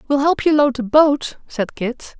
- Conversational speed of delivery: No, fast, 220 wpm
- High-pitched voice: Yes, very high, 275 Hz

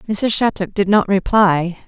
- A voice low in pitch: No, high, 195 Hz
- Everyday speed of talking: Yes, average, 160 wpm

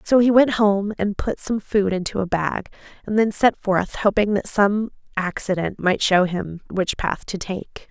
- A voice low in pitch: No, high, 200 Hz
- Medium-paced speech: Yes, average, 195 wpm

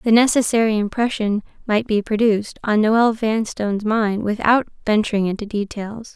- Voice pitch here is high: Yes, high, 215 Hz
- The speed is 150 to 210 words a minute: No, slow, 135 wpm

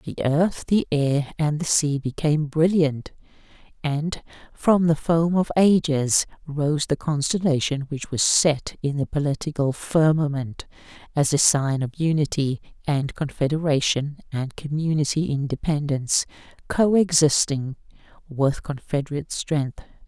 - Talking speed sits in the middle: No, slow, 115 wpm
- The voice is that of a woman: Yes, female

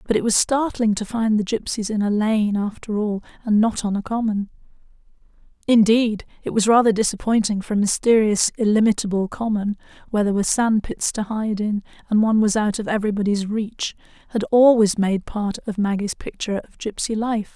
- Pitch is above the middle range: Yes, high, 215 Hz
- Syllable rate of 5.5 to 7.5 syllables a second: Yes, 5.6 syllables/s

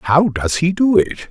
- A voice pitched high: No, medium, 165 Hz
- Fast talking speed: Yes, fast, 230 wpm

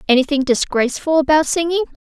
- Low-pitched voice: No, very high, 290 Hz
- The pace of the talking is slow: Yes, slow, 120 wpm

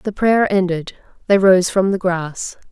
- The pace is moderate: Yes, average, 175 wpm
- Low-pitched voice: No, high, 190 Hz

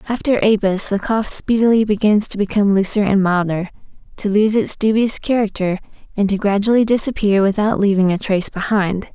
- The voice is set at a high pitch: Yes, high, 205 Hz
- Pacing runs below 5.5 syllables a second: No, 5.7 syllables/s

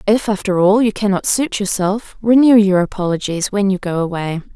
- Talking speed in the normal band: Yes, average, 185 wpm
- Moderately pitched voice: No, high, 200 Hz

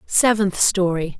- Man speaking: No, female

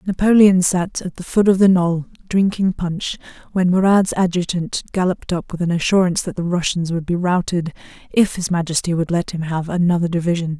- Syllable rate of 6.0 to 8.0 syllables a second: No, 5.5 syllables/s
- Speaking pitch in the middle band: Yes, medium, 175 Hz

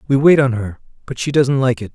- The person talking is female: No, male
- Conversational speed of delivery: No, fast, 275 wpm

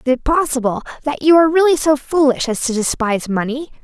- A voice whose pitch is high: Yes, very high, 275 Hz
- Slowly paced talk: No, fast, 205 wpm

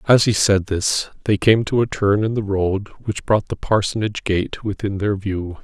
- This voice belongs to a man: Yes, male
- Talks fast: Yes, fast, 215 wpm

